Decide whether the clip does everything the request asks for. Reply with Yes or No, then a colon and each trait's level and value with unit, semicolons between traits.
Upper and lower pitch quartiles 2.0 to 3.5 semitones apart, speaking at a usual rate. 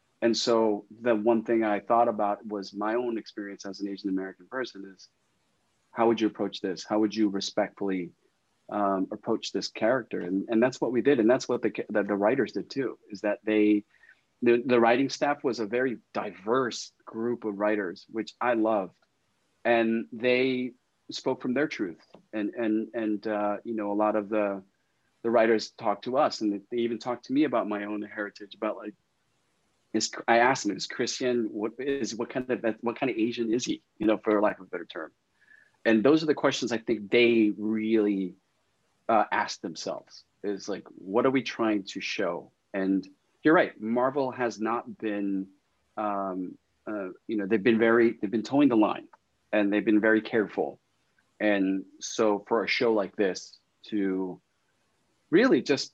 Yes: narrow, 2.4 semitones; average, 185 wpm